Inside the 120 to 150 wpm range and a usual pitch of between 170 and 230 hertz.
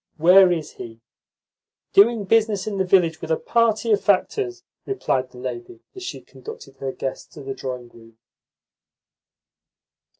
Yes: average, 145 wpm; medium, 185 Hz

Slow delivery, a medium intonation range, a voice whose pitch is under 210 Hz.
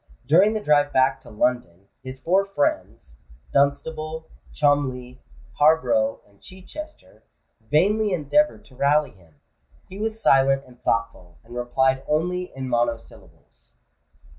No: slow, 115 wpm; wide, 6.7 semitones; medium, 140 Hz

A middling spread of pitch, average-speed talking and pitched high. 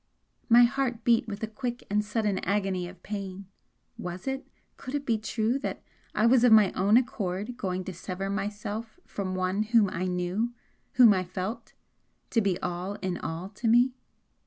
Yes: average, 3.9 semitones; average, 180 wpm; high, 210 Hz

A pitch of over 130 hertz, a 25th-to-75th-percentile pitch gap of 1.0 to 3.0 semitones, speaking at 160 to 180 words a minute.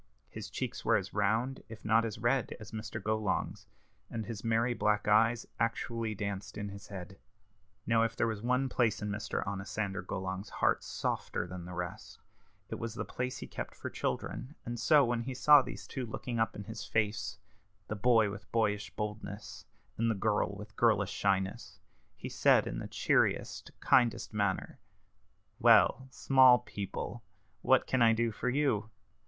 No: low, 110 Hz; narrow, 2.5 semitones; average, 170 wpm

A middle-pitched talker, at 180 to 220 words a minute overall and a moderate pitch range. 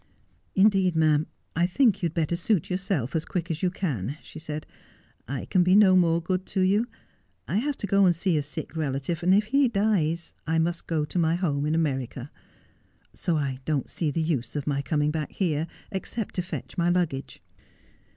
Yes: medium, 170 Hz; average, 200 wpm; average, 3.8 semitones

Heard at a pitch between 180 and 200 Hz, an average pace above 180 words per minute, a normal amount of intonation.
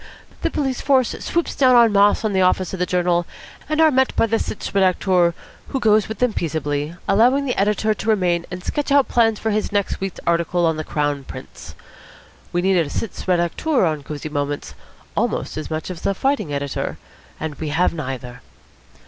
No: medium, 185 Hz; average, 195 wpm; wide, 5.8 semitones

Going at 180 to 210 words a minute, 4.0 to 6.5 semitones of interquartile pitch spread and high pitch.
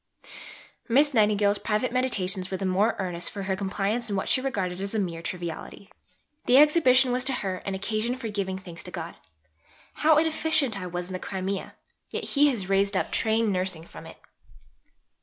Yes: average, 185 wpm; average, 4.7 semitones; high, 200 Hz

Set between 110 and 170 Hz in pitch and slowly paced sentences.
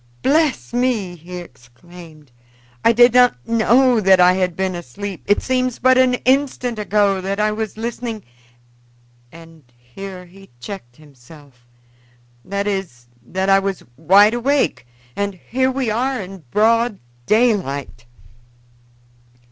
No: high, 200 Hz; slow, 130 wpm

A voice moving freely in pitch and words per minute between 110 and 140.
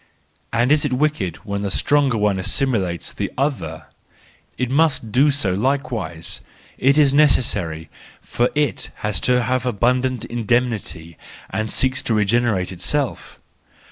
No: average, 5.0 semitones; slow, 135 wpm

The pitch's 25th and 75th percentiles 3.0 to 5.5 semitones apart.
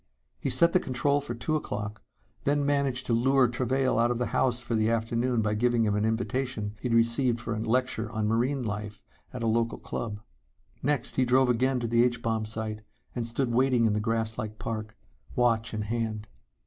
No: narrow, 2.4 semitones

